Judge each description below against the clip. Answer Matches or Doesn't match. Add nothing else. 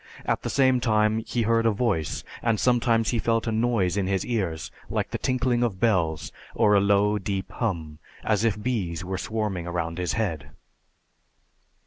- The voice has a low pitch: Matches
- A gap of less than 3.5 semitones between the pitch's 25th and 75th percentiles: Doesn't match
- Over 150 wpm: Matches